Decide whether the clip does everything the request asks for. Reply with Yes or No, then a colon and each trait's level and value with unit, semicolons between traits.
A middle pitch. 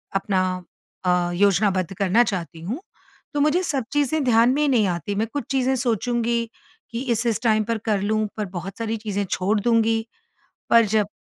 No: high, 220 Hz